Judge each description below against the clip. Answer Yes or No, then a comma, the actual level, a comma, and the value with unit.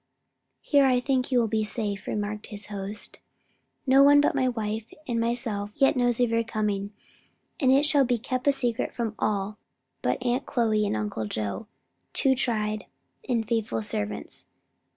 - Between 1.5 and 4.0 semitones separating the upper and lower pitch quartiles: Yes, average, 3.4 semitones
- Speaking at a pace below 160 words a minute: No, average, 165 wpm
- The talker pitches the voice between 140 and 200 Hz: No, high, 230 Hz